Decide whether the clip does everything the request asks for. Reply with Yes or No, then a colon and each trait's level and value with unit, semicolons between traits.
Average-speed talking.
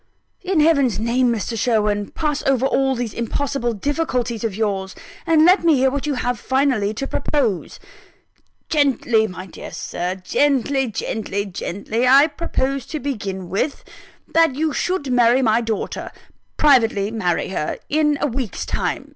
Yes: average, 150 wpm